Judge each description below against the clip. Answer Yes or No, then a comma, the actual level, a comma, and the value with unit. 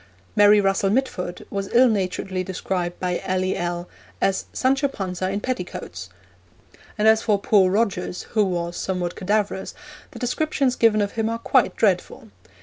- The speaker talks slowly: No, average, 145 wpm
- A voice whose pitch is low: No, high, 195 Hz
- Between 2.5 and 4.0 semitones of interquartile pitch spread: Yes, average, 3.3 semitones